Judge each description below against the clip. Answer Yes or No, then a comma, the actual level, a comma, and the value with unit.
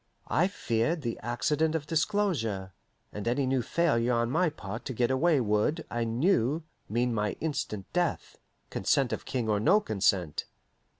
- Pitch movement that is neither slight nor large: No, wide, 6.2 semitones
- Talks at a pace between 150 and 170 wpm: Yes, average, 160 wpm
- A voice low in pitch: Yes, low, 125 Hz